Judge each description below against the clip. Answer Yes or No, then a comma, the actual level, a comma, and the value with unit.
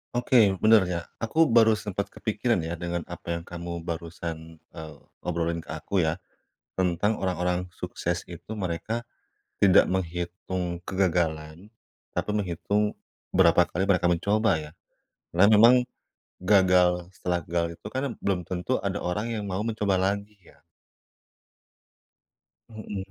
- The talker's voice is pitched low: Yes, very low, 90 Hz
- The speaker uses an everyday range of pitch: Yes, average, 3.2 semitones